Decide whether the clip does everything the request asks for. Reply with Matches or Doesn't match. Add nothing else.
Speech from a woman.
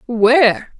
Matches